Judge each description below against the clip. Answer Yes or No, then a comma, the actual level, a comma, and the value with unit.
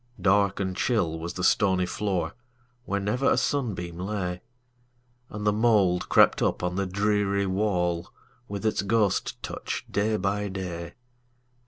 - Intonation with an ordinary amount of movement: Yes, average, 3.8 semitones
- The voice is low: Yes, low, 100 Hz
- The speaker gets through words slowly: Yes, slow, 130 wpm